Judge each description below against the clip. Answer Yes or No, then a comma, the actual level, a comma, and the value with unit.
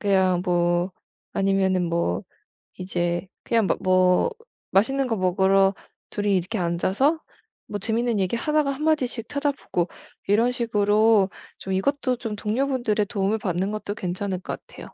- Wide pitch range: No, average, 4.1 semitones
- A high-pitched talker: Yes, high, 200 Hz